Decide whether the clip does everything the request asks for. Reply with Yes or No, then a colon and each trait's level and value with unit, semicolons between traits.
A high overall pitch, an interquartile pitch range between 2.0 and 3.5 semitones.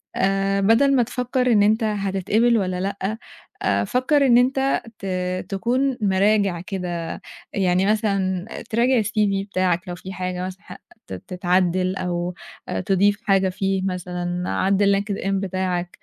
Yes: high, 195 Hz; average, 2.8 semitones